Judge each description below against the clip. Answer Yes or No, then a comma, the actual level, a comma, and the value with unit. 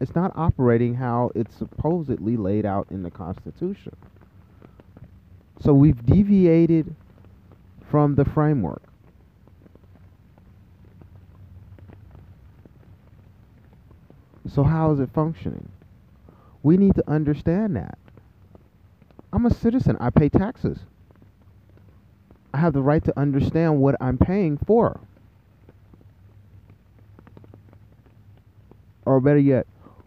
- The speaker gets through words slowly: Yes, slow, 90 wpm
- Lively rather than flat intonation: Yes, wide, 6.1 semitones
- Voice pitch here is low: Yes, low, 105 Hz